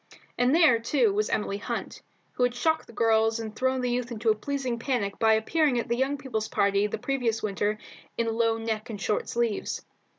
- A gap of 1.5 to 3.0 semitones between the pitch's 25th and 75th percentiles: Yes, narrow, 2.5 semitones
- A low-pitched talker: No, high, 230 Hz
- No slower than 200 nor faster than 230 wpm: Yes, fast, 205 wpm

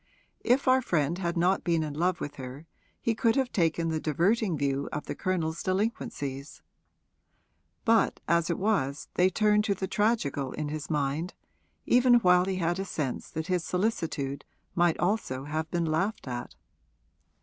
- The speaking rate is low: No, average, 165 wpm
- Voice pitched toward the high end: No, medium, 170 Hz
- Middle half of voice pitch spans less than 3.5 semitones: No, average, 4.7 semitones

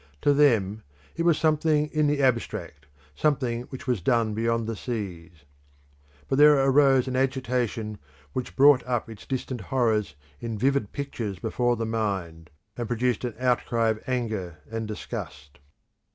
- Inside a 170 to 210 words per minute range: No, average, 150 wpm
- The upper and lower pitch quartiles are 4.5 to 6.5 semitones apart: No, average, 3.6 semitones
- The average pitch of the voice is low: Yes, low, 120 Hz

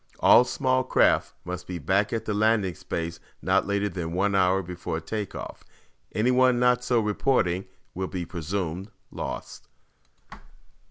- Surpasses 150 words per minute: No, average, 145 wpm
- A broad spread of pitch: No, average, 3.8 semitones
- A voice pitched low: Yes, very low, 95 Hz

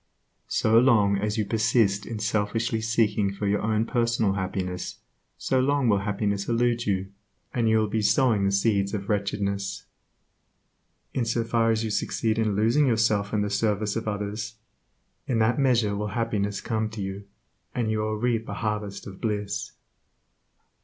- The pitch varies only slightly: Yes, narrow, 2.0 semitones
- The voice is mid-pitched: No, low, 110 Hz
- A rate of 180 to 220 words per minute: No, average, 165 wpm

